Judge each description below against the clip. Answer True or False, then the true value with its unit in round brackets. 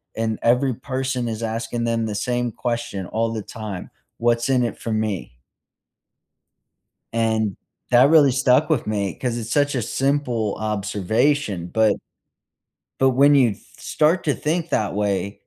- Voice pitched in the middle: False (115 Hz)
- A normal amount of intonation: True (3.5 semitones)